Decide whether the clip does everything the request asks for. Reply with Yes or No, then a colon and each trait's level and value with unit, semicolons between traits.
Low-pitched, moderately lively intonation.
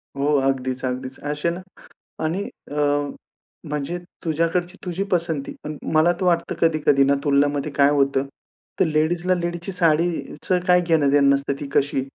No: medium, 150 Hz; average, 3.4 semitones